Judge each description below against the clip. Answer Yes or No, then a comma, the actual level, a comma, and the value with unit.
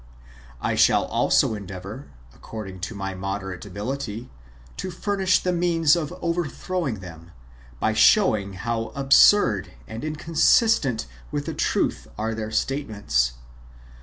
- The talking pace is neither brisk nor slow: No, slow, 120 wpm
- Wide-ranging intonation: Yes, wide, 8.5 semitones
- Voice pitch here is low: Yes, low, 110 Hz